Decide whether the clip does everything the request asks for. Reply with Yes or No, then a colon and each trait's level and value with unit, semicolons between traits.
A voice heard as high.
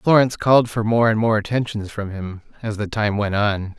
No: low, 110 Hz